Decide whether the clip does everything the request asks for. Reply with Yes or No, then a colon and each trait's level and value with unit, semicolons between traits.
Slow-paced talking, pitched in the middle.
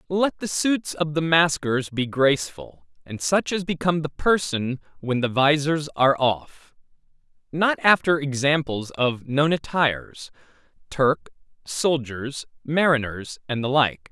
Yes: slow, 130 wpm; medium, 145 Hz